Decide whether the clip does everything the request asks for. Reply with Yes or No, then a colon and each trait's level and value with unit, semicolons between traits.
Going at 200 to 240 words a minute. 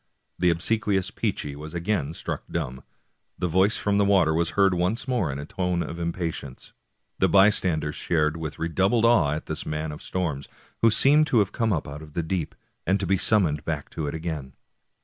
Yes: fast, 205 wpm